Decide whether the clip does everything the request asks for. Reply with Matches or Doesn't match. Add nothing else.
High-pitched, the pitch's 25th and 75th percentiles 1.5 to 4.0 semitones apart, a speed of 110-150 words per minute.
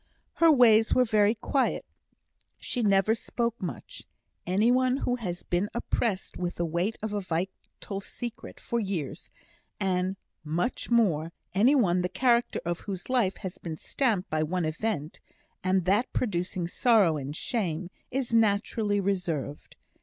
Doesn't match